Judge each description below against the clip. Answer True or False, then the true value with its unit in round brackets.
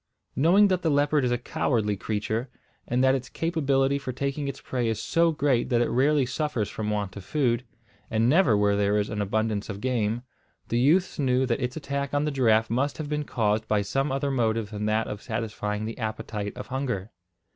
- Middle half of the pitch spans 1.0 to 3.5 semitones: False (4.5 semitones)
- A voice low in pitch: True (125 Hz)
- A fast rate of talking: True (210 wpm)